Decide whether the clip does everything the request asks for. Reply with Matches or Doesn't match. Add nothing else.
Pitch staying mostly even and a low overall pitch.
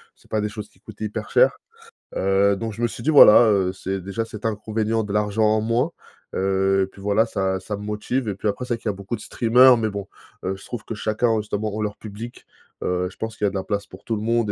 Matches